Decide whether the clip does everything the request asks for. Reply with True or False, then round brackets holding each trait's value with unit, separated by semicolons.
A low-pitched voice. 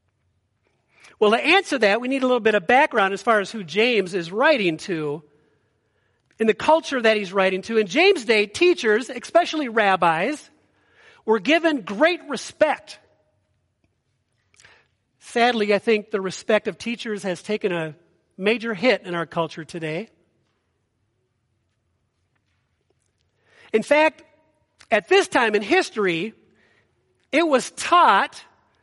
False (215 Hz)